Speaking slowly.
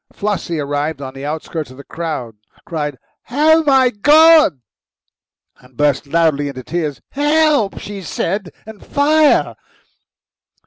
Yes: slow, 125 wpm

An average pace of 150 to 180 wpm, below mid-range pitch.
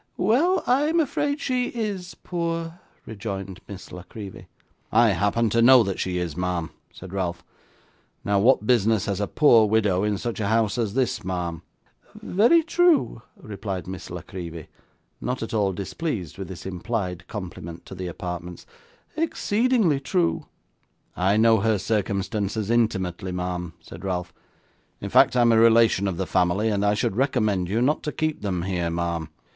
Yes: average, 165 wpm; low, 105 Hz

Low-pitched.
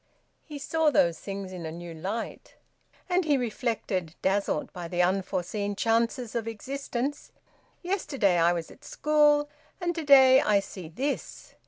No: high, 225 Hz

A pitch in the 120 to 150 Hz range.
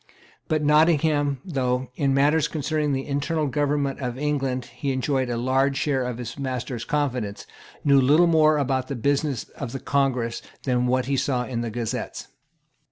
Yes: low, 135 Hz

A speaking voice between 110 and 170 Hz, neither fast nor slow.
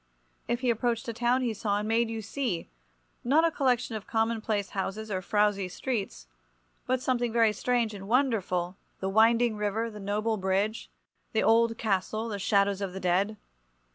No: high, 220 Hz; average, 170 wpm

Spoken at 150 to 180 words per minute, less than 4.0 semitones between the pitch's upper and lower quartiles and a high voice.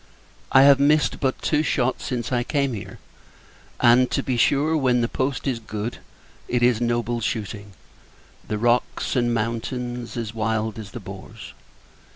No: average, 160 wpm; narrow, 2.6 semitones; low, 120 Hz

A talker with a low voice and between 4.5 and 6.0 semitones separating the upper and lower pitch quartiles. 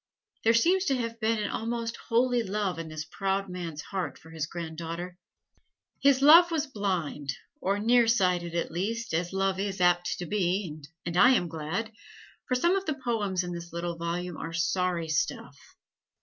No: high, 190 Hz; average, 5.2 semitones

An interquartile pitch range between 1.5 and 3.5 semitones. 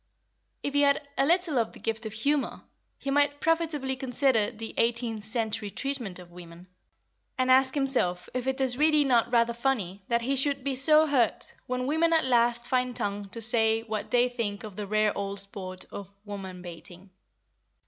No: average, 4.7 semitones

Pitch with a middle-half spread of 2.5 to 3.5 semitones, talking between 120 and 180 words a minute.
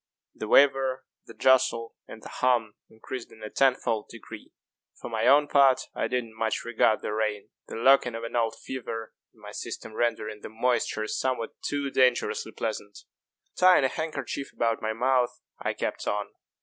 Yes: average, 2.9 semitones; average, 175 wpm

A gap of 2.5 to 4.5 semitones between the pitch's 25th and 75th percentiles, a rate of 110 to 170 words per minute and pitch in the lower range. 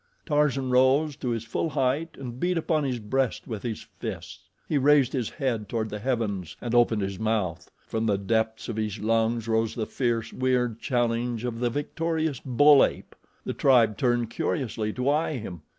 No: average, 3.4 semitones; average, 180 wpm; low, 120 Hz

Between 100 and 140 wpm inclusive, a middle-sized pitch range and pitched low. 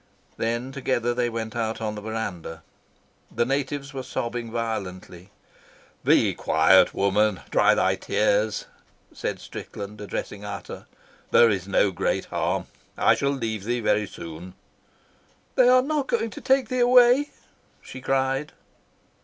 Yes: slow, 135 wpm; average, 4.8 semitones; low, 115 Hz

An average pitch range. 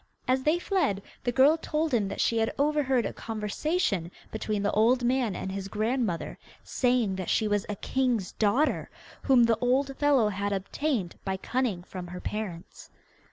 Yes: average, 4.9 semitones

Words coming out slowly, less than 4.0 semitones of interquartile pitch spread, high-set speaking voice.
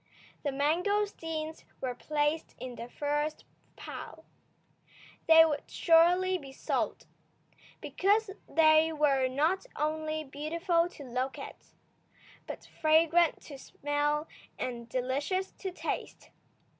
Yes: slow, 105 wpm; average, 2.9 semitones; very high, 310 Hz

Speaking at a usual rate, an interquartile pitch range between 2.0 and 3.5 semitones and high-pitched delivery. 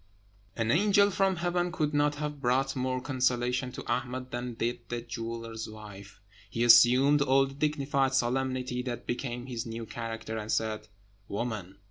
No: average, 155 wpm; average, 3.0 semitones; low, 125 Hz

